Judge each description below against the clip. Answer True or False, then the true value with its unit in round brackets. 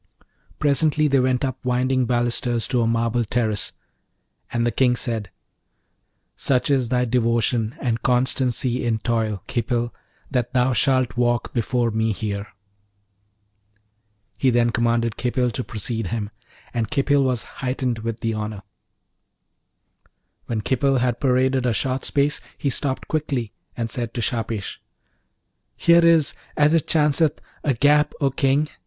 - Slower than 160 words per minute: True (140 wpm)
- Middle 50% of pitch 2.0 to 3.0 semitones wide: True (2.4 semitones)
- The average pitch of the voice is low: True (125 Hz)